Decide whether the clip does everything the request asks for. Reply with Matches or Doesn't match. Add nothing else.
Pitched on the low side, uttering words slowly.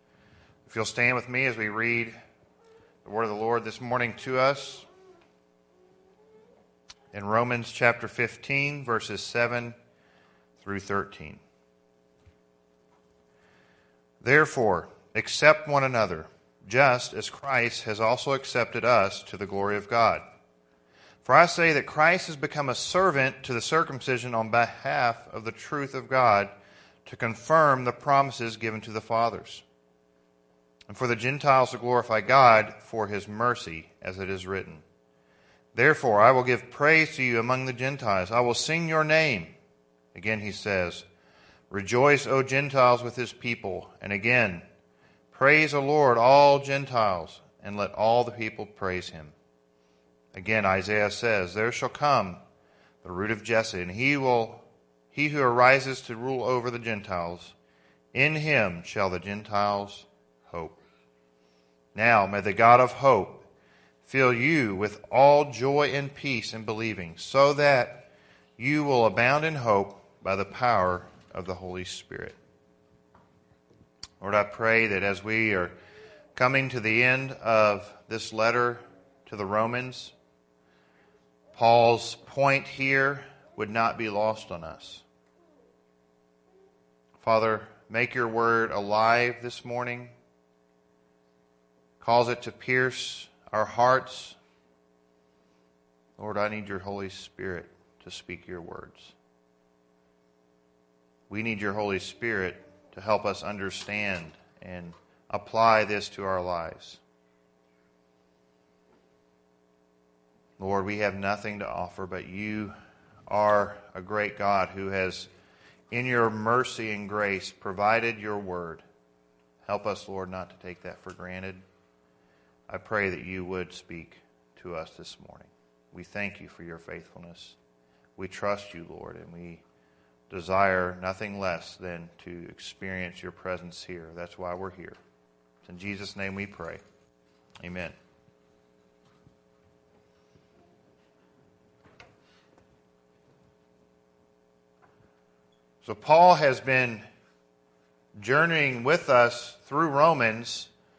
Matches